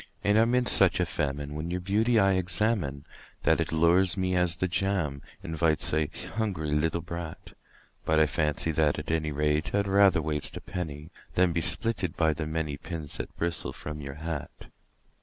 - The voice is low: Yes, very low, 80 Hz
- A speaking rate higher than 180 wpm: Yes, average, 190 wpm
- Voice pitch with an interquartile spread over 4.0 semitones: No, average, 3.5 semitones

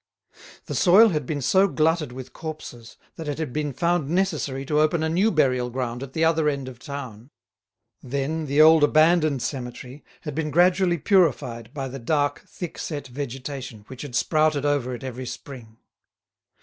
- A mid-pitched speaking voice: Yes, medium, 145 Hz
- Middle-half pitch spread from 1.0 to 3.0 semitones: No, average, 3.6 semitones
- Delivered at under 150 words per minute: No, average, 175 wpm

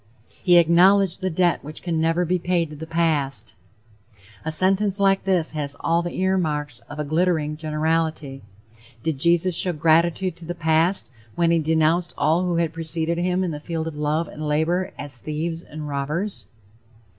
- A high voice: No, medium, 165 Hz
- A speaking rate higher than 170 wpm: Yes, average, 180 wpm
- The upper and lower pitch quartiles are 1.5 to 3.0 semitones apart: Yes, narrow, 2.5 semitones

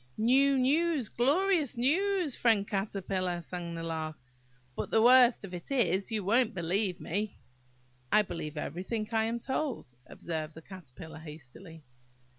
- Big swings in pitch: Yes, wide, 6.9 semitones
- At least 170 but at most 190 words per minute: No, average, 140 wpm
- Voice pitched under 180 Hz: No, high, 205 Hz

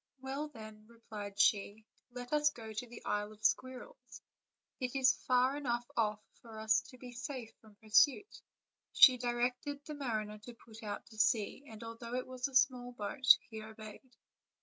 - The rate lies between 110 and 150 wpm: No, average, 175 wpm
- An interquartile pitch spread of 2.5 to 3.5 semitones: Yes, average, 3.0 semitones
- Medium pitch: No, high, 240 Hz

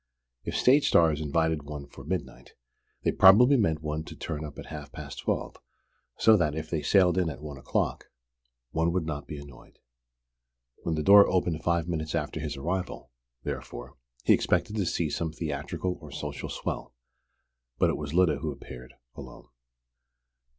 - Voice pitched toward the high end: No, very low, 80 Hz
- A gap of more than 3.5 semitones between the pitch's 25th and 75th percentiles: No, average, 3.2 semitones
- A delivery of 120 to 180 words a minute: Yes, average, 170 wpm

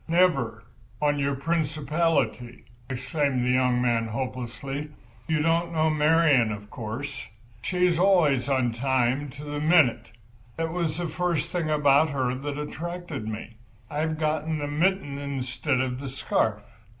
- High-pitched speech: No, medium, 145 Hz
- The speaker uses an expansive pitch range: No, average, 3.9 semitones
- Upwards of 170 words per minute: No, average, 140 wpm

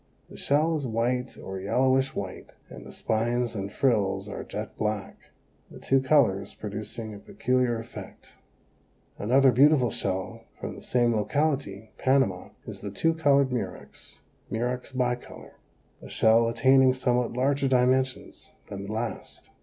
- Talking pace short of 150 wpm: Yes, average, 140 wpm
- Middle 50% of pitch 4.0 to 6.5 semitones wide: No, average, 3.5 semitones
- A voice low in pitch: Yes, low, 125 Hz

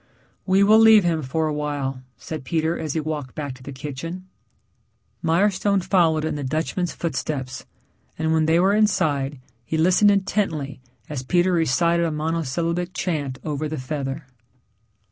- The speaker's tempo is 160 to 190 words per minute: No, average, 150 wpm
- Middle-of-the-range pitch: Yes, medium, 160 Hz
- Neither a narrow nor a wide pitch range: Yes, average, 3.6 semitones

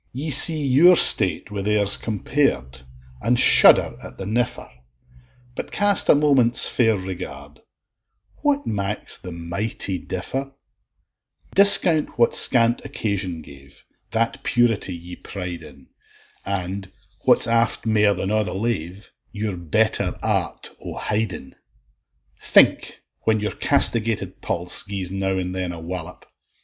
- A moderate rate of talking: No, slow, 130 wpm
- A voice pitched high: No, low, 100 Hz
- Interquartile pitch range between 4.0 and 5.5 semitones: Yes, average, 4.6 semitones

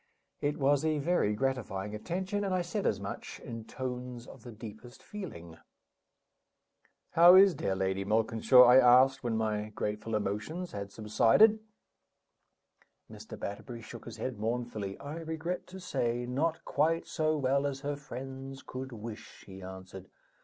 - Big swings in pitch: Yes, wide, 6.0 semitones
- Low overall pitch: Yes, low, 125 Hz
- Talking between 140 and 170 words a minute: Yes, average, 150 wpm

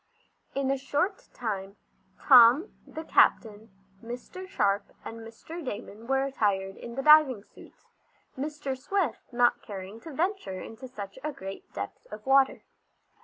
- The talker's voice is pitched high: Yes, very high, 250 Hz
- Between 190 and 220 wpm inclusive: No, average, 140 wpm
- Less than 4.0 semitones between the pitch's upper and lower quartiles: No, average, 5.3 semitones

